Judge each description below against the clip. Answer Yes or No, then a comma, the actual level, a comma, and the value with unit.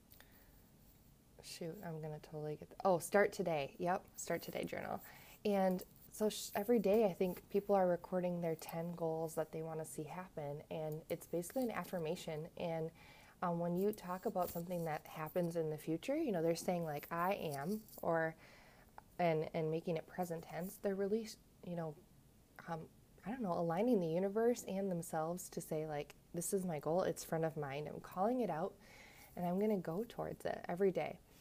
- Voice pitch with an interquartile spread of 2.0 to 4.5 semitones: Yes, average, 3.4 semitones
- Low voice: No, medium, 175 Hz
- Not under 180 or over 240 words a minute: Yes, average, 185 wpm